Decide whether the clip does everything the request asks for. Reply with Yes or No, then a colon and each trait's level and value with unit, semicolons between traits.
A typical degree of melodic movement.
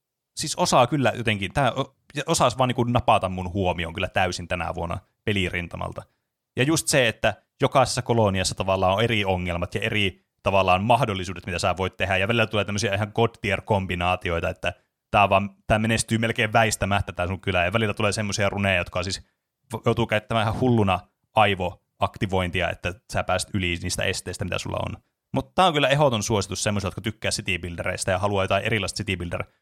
Yes: average, 3.6 semitones